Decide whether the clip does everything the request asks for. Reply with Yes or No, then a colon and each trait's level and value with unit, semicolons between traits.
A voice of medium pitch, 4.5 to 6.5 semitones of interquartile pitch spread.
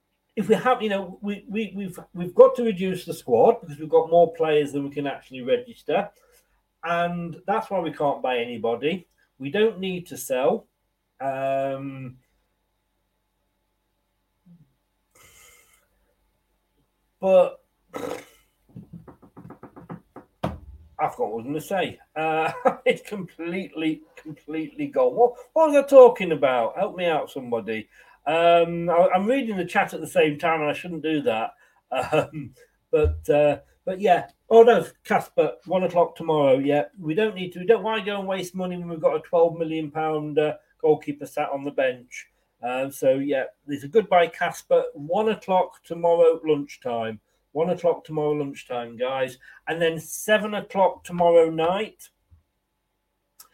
Yes: medium, 165 Hz; wide, 5.5 semitones